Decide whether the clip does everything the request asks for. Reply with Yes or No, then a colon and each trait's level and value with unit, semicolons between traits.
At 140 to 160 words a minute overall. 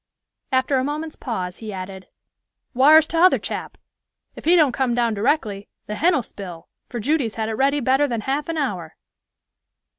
No: average, 170 wpm